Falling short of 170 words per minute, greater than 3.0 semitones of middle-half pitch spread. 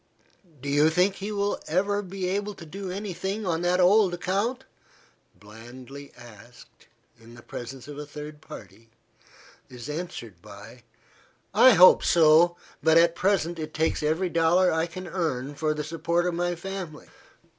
Yes: average, 160 wpm; average, 4.1 semitones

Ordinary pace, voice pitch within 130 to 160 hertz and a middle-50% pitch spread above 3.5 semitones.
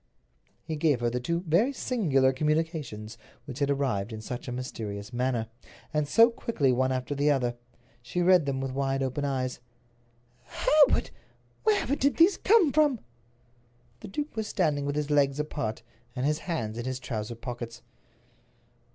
Yes: average, 160 wpm; medium, 140 Hz; average, 5.2 semitones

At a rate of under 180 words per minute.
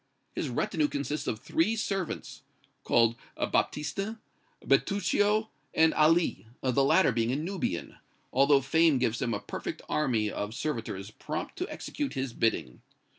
Yes: slow, 135 wpm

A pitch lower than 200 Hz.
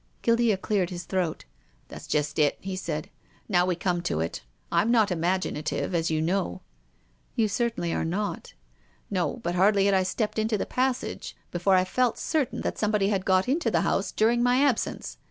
Yes: high, 190 Hz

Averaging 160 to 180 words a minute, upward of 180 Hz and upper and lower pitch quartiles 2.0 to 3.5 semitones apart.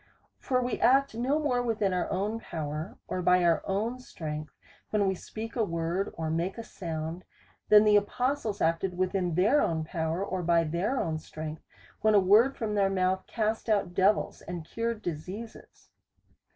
No: average, 175 wpm; high, 190 Hz; average, 4.8 semitones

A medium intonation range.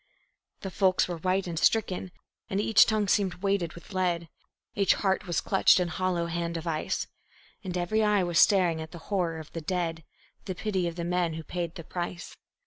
No: narrow, 2.2 semitones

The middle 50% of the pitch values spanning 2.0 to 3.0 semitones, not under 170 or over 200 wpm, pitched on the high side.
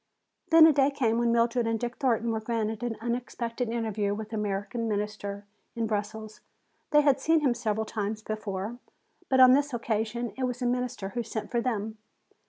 Yes: narrow, 2.4 semitones; average, 190 wpm; high, 230 Hz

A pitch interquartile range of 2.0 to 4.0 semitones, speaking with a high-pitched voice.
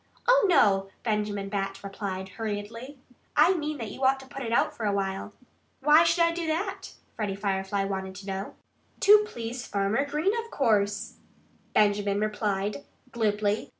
No: wide, 5.5 semitones; high, 210 Hz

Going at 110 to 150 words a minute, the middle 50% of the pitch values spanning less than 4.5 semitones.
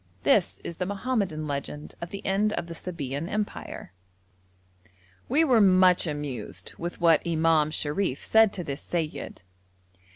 No: average, 140 wpm; average, 4.8 semitones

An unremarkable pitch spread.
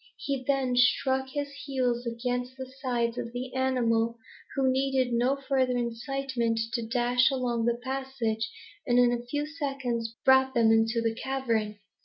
No: narrow, 2.1 semitones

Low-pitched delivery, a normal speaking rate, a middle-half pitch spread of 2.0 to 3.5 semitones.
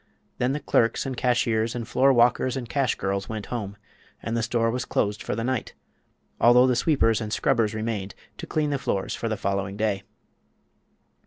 Yes: low, 115 Hz; average, 180 wpm; average, 2.8 semitones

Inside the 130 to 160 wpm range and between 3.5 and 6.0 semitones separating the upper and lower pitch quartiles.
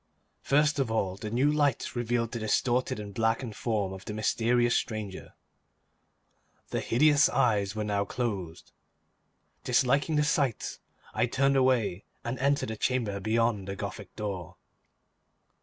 Yes: average, 140 wpm; average, 3.8 semitones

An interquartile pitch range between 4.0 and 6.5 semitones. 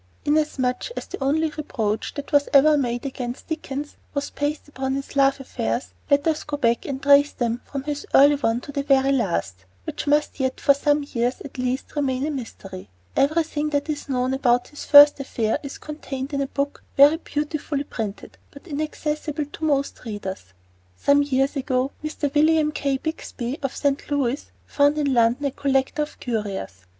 No: narrow, 2.6 semitones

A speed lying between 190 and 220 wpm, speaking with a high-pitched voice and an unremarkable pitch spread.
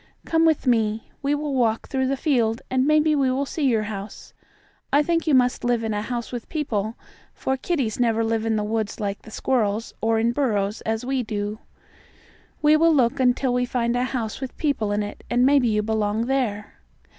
Yes: fast, 205 wpm; high, 240 Hz; average, 3.6 semitones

